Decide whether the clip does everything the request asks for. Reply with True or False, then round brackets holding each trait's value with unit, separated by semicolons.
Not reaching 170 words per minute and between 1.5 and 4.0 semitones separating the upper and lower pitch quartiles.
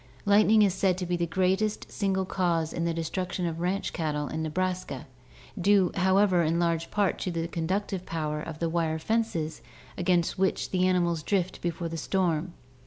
False (175 wpm; 2.4 semitones)